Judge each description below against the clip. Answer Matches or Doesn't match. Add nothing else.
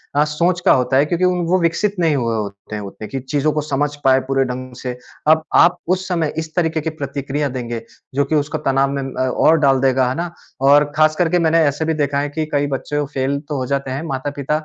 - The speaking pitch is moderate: Matches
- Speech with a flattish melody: Doesn't match